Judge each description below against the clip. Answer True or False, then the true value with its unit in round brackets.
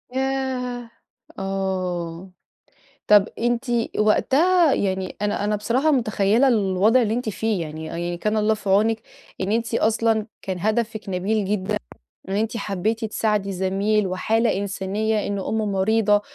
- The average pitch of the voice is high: True (210 Hz)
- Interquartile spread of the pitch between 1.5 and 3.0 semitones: True (2.7 semitones)